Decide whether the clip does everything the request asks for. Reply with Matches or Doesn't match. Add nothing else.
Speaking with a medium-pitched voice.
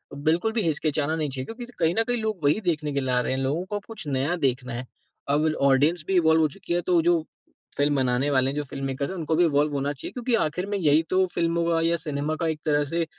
Matches